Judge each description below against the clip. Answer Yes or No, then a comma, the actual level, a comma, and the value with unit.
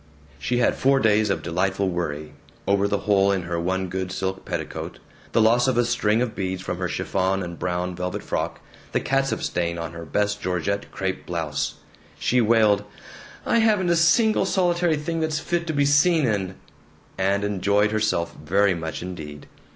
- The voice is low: Yes, low, 100 Hz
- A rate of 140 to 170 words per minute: No, average, 180 wpm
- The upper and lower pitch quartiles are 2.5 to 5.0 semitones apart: No, wide, 5.4 semitones